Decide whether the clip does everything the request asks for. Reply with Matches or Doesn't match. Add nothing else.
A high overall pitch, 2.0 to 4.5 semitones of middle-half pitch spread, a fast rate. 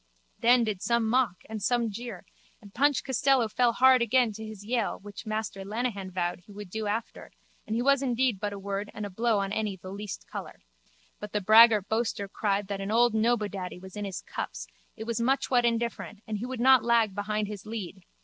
Matches